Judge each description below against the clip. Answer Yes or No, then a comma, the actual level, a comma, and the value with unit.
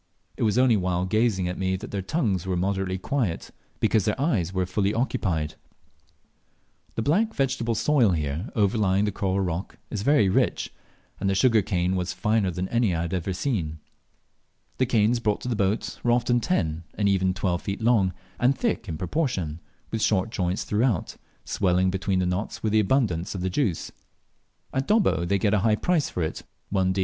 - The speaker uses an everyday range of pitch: Yes, average, 4.1 semitones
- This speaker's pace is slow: No, average, 190 wpm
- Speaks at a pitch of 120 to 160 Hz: No, low, 100 Hz